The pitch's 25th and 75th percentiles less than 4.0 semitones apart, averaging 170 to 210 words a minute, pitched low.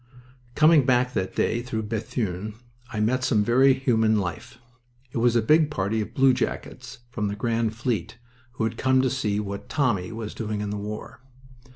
Yes: average, 3.4 semitones; average, 180 wpm; low, 115 Hz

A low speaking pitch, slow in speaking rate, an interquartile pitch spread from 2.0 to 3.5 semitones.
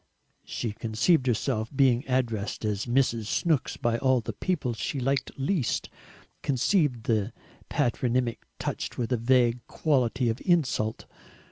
Yes: low, 125 Hz; slow, 130 wpm; average, 2.9 semitones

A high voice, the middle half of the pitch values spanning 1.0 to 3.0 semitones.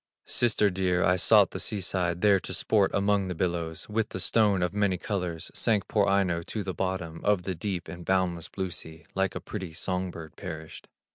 No: very low, 95 Hz; narrow, 2.5 semitones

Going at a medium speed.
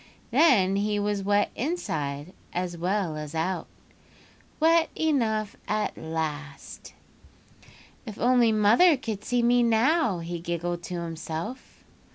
No: slow, 115 wpm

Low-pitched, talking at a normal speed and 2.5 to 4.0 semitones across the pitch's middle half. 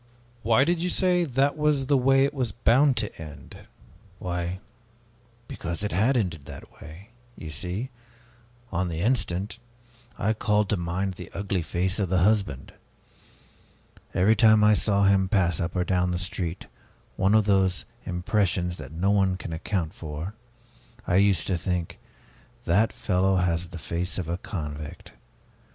Yes: very low, 95 Hz; average, 160 wpm; average, 3.7 semitones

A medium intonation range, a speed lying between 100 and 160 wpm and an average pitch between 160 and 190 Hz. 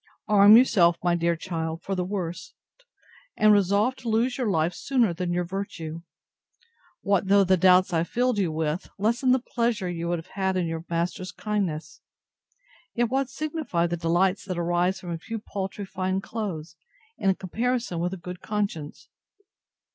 No: average, 3.6 semitones; average, 170 wpm; medium, 185 Hz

